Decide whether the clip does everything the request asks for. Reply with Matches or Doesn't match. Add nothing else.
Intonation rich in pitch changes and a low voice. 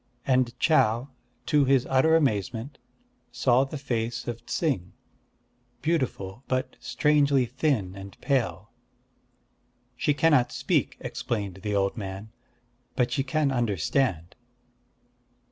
Doesn't match